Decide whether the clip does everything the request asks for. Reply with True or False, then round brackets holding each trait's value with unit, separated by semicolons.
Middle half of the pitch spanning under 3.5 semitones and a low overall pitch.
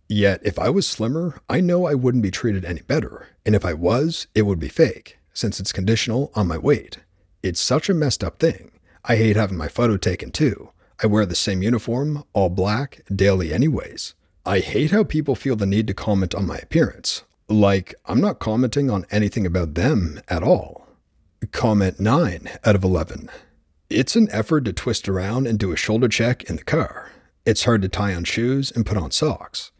False (4.8 semitones; 105 Hz)